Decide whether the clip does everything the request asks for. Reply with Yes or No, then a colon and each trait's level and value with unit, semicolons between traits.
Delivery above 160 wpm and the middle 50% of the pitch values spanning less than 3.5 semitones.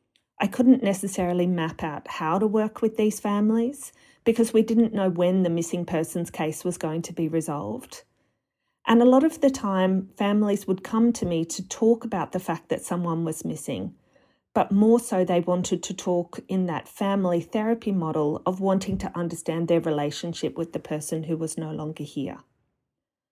No: average, 185 wpm; average, 4.3 semitones